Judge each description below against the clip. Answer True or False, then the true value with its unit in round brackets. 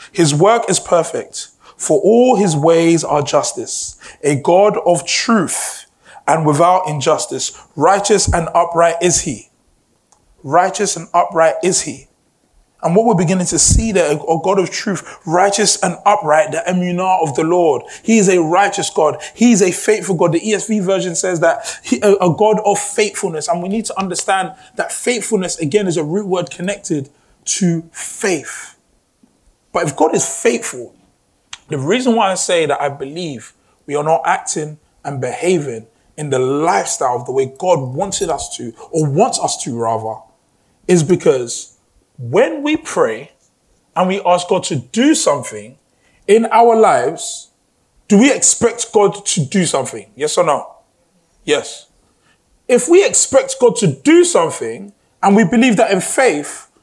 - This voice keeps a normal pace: True (160 wpm)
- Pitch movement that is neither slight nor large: True (4.7 semitones)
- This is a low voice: False (180 Hz)